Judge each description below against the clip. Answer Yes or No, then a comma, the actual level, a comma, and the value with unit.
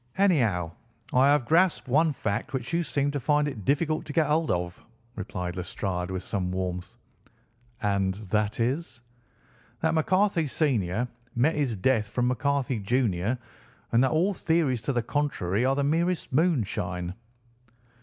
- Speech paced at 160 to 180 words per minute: No, average, 150 wpm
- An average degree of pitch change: No, wide, 7.1 semitones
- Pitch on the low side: Yes, low, 125 Hz